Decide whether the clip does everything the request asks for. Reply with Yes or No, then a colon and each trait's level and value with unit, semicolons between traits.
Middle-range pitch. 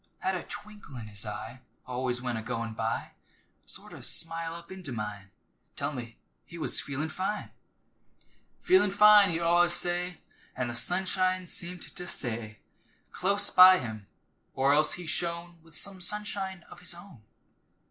Yes: medium, 170 Hz